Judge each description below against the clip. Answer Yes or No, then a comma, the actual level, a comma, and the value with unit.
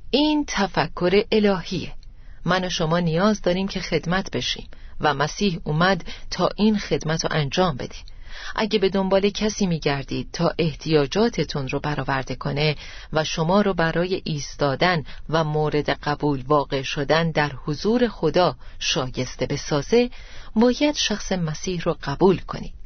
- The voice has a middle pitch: Yes, medium, 165 Hz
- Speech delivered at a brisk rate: No, average, 135 wpm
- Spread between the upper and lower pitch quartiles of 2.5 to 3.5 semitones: No, average, 4.7 semitones